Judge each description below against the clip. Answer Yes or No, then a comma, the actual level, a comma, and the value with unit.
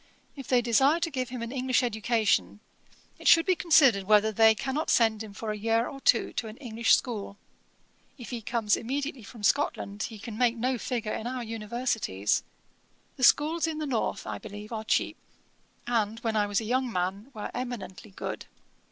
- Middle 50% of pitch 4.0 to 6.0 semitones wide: No, average, 3.1 semitones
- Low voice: No, high, 230 Hz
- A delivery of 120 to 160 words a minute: No, average, 190 wpm